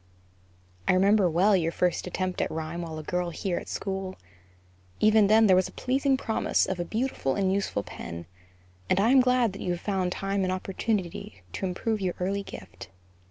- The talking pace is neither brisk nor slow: Yes, average, 195 wpm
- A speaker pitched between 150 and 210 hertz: Yes, high, 190 Hz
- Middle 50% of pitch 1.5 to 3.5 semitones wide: Yes, average, 3.1 semitones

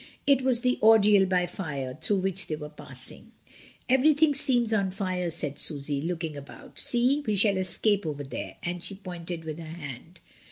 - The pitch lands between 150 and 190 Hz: Yes, medium, 185 Hz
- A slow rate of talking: No, average, 175 wpm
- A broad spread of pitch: Yes, wide, 5.8 semitones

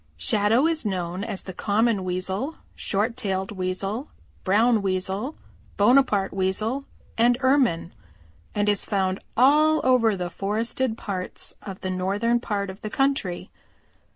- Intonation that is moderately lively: Yes, average, 4.2 semitones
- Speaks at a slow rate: Yes, slow, 130 wpm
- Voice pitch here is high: Yes, high, 205 Hz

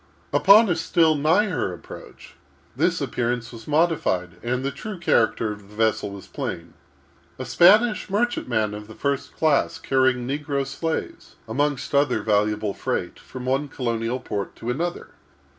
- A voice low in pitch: Yes, low, 130 Hz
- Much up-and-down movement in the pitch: Yes, wide, 6.3 semitones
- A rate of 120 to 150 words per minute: Yes, average, 140 wpm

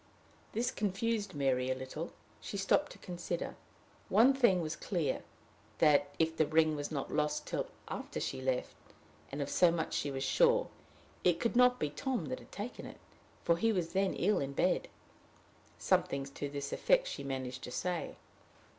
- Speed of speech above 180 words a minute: No, average, 175 wpm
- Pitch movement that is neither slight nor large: No, wide, 6.8 semitones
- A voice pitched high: No, medium, 165 Hz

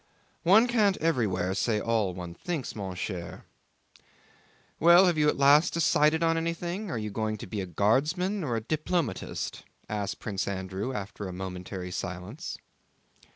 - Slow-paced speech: No, average, 155 wpm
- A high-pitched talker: No, low, 115 Hz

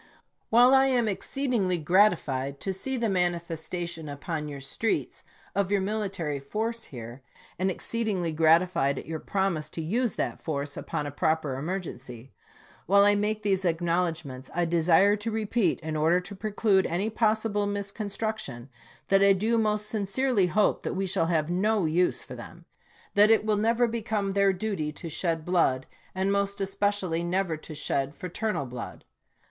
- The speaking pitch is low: No, high, 190 Hz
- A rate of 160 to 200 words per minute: Yes, average, 165 wpm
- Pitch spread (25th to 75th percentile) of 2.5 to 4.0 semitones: No, average, 4.7 semitones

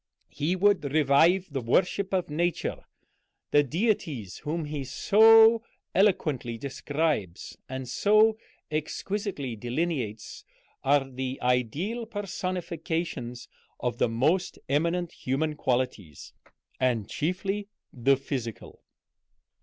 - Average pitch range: No, wide, 6.3 semitones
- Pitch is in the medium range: Yes, medium, 150 Hz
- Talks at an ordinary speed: No, slow, 100 wpm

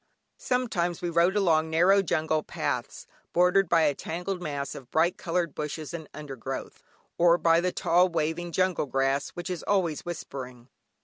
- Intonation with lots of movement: No, average, 2.7 semitones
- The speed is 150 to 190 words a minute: Yes, average, 160 wpm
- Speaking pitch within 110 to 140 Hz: No, medium, 170 Hz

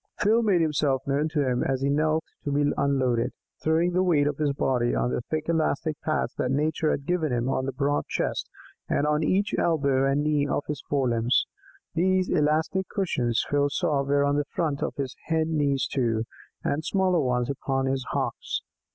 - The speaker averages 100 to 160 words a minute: No, average, 195 wpm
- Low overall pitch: No, medium, 145 Hz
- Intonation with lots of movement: No, average, 2.8 semitones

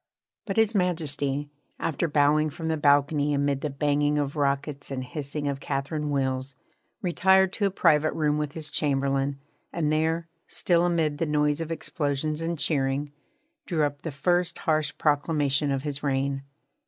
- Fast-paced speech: No, average, 160 wpm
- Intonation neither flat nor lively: No, narrow, 2.3 semitones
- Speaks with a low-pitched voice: No, medium, 150 Hz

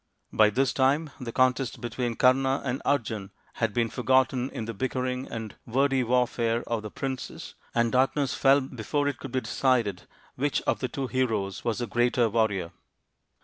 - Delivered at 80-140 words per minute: No, average, 170 wpm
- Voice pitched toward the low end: Yes, low, 125 Hz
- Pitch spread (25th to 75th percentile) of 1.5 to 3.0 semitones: Yes, narrow, 2.6 semitones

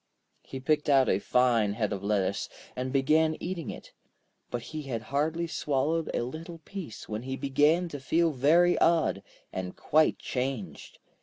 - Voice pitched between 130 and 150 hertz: Yes, low, 135 Hz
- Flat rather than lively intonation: No, average, 5.0 semitones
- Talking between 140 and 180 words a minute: Yes, average, 160 wpm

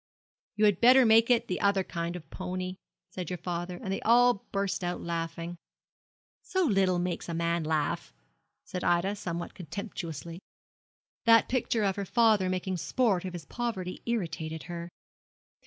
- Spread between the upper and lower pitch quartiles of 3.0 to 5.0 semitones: Yes, average, 3.7 semitones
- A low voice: No, medium, 185 Hz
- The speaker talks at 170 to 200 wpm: No, average, 160 wpm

